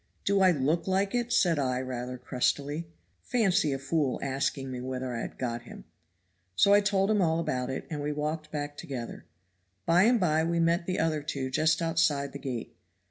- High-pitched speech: No, medium, 150 Hz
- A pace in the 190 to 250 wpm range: Yes, average, 195 wpm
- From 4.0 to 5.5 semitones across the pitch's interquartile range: Yes, average, 4.6 semitones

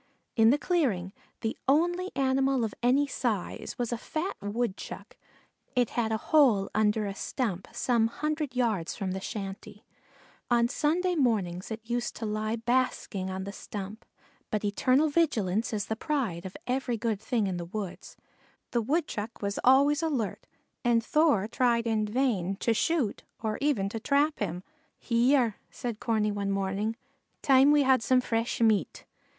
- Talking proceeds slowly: No, average, 160 wpm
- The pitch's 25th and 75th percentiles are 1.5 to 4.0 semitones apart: No, average, 4.4 semitones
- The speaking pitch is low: No, high, 230 Hz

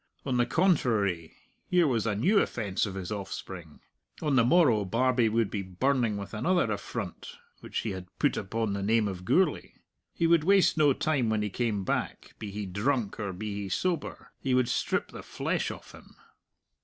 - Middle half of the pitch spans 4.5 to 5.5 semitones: Yes, average, 5.2 semitones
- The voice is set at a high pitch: No, low, 115 Hz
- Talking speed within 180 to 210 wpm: Yes, average, 190 wpm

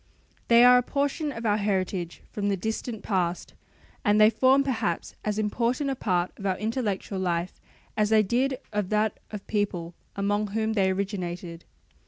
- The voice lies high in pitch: Yes, high, 210 Hz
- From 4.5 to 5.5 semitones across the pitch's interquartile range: No, average, 3.4 semitones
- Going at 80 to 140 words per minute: No, average, 175 wpm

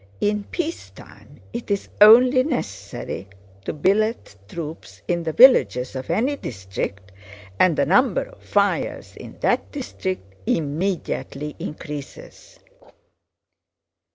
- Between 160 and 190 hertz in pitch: Yes, medium, 185 Hz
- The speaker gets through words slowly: Yes, slow, 105 wpm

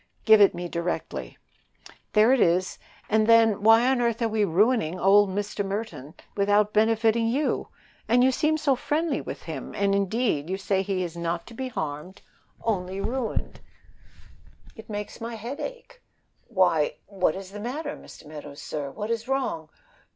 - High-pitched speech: Yes, high, 210 Hz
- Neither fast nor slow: Yes, average, 165 wpm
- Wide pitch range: No, average, 4.2 semitones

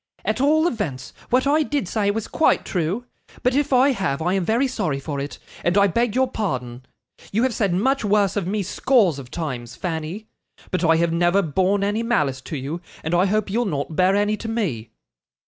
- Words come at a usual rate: No, fast, 210 wpm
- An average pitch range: No, wide, 5.9 semitones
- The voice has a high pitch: Yes, high, 195 Hz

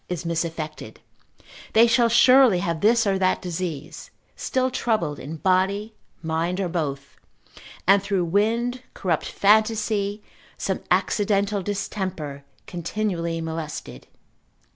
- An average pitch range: Yes, average, 4.3 semitones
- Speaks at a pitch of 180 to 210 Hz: Yes, high, 190 Hz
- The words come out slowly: Yes, slow, 110 wpm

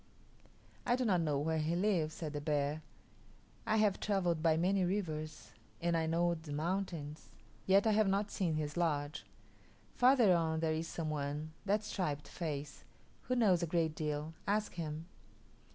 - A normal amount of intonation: Yes, average, 3.9 semitones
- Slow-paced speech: No, average, 170 wpm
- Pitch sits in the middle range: Yes, medium, 165 Hz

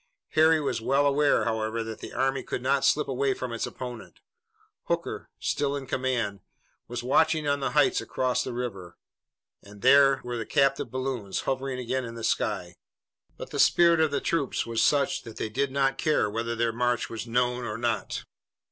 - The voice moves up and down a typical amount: Yes, average, 3.2 semitones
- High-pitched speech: No, low, 125 Hz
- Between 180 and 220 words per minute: Yes, average, 185 wpm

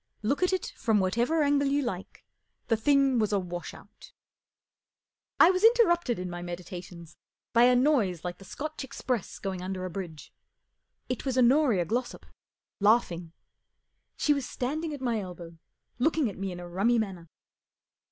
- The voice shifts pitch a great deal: Yes, wide, 7.4 semitones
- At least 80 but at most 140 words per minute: No, average, 165 wpm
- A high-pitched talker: Yes, high, 225 Hz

